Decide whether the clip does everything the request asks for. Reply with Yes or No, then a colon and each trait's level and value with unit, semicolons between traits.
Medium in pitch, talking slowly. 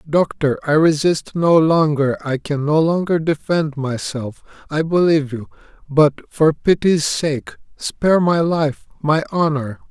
Yes: medium, 155 Hz; slow, 125 wpm